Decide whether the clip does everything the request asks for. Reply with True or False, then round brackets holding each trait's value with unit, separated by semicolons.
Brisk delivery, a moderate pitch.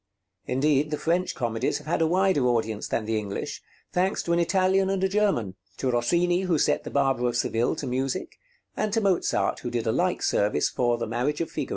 True (215 wpm; 145 Hz)